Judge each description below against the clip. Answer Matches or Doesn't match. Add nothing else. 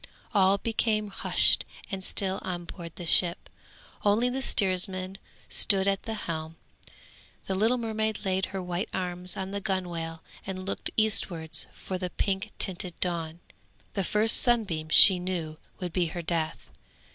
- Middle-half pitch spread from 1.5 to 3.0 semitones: Matches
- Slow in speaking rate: Doesn't match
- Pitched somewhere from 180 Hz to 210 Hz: Matches